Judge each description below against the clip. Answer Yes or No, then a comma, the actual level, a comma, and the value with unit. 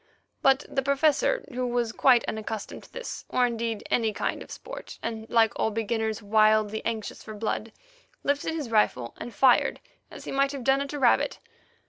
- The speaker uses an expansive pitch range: No, average, 3.6 semitones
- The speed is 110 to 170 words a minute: No, average, 180 wpm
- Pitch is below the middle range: No, high, 230 Hz